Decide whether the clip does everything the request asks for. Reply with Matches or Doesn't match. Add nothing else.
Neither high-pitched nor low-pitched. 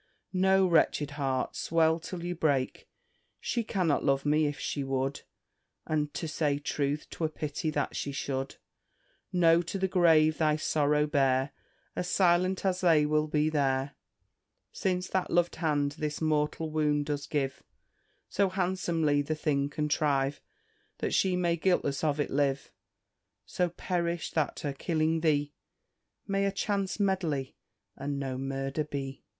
Matches